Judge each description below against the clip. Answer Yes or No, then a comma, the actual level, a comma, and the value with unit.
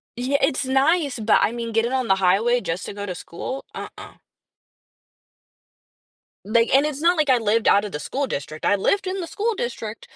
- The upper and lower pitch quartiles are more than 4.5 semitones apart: Yes, wide, 5.4 semitones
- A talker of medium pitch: No, high, 240 Hz